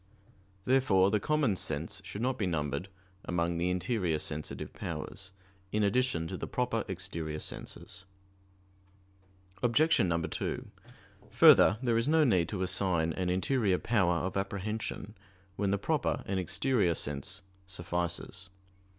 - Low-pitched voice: Yes, very low, 95 Hz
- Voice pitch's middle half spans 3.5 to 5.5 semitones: Yes, average, 3.9 semitones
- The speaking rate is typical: No, slow, 130 wpm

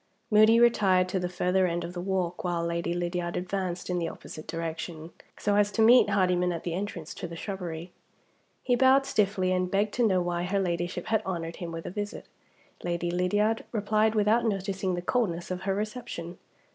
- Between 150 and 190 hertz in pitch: Yes, medium, 185 Hz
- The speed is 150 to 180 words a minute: No, average, 195 wpm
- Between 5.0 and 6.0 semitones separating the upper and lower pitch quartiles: No, average, 3.0 semitones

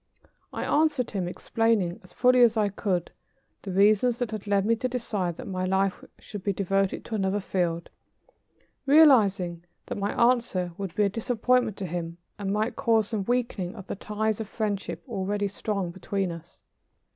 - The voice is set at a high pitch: Yes, high, 200 Hz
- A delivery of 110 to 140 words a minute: No, average, 175 wpm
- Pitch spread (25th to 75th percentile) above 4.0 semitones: No, average, 3.3 semitones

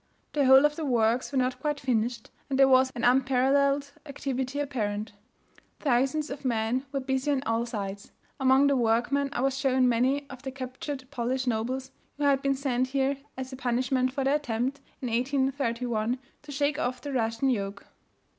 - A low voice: No, very high, 260 Hz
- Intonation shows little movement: Yes, narrow, 2.2 semitones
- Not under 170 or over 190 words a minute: Yes, average, 180 wpm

